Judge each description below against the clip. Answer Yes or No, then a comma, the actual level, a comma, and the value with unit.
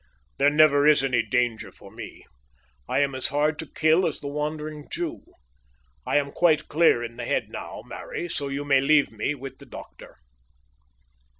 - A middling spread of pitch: No, narrow, 2.2 semitones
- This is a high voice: No, medium, 145 Hz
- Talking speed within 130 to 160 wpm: No, average, 180 wpm